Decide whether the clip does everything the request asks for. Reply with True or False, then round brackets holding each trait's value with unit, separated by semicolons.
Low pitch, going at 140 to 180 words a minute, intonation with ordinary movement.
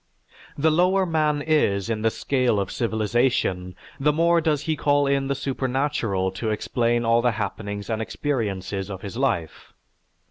False (120 Hz; 155 wpm; 6.0 semitones)